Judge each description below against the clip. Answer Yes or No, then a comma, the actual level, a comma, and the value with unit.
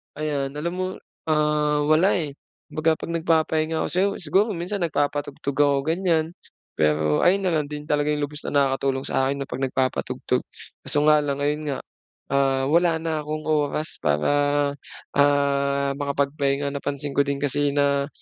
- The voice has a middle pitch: Yes, medium, 145 Hz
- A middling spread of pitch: No, narrow, 2.0 semitones